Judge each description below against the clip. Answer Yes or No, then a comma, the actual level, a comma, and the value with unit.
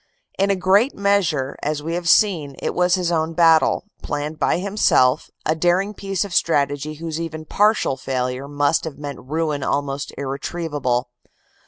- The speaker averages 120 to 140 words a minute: No, average, 160 wpm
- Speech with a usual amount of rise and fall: Yes, average, 4.0 semitones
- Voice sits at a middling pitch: Yes, medium, 160 Hz